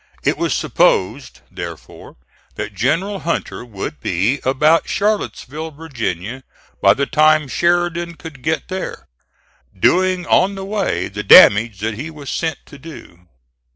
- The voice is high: No, medium, 150 Hz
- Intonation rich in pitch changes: Yes, wide, 6.5 semitones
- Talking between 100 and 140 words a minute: Yes, slow, 135 wpm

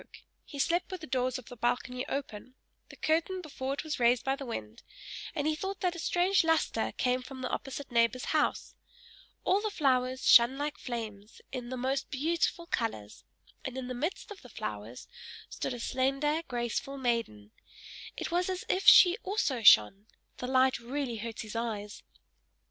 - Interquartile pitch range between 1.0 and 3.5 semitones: No, average, 4.7 semitones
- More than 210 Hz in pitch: Yes, very high, 260 Hz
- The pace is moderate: Yes, average, 190 wpm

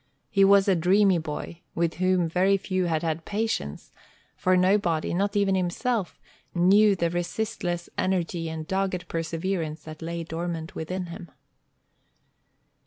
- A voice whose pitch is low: No, medium, 180 Hz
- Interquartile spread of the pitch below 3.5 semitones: Yes, average, 2.7 semitones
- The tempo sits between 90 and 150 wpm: Yes, slow, 135 wpm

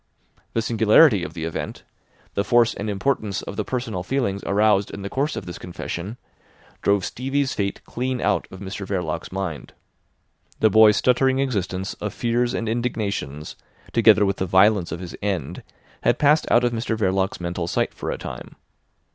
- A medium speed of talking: Yes, average, 170 wpm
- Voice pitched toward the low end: Yes, low, 105 Hz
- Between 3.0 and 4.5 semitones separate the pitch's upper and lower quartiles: Yes, average, 4.2 semitones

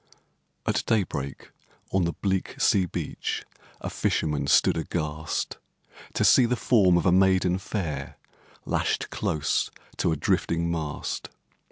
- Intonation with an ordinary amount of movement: Yes, average, 3.5 semitones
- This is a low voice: Yes, very low, 85 Hz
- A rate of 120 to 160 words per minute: Yes, slow, 135 wpm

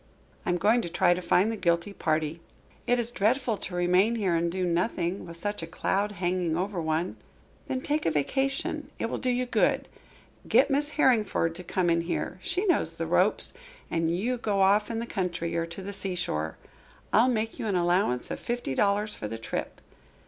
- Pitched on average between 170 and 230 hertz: Yes, high, 190 Hz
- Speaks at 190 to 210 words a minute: Yes, average, 200 wpm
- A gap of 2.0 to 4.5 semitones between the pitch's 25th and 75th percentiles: No, average, 5.1 semitones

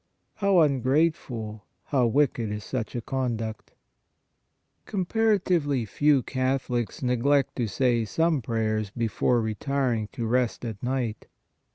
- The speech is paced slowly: Yes, slow, 125 wpm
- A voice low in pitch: Yes, low, 125 Hz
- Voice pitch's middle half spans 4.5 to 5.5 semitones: No, average, 4.0 semitones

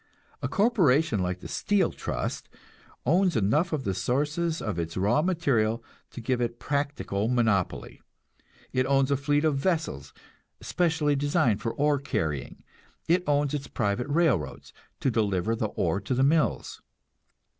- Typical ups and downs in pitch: No, wide, 6.0 semitones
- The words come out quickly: No, average, 145 wpm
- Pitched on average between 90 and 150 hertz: Yes, low, 135 Hz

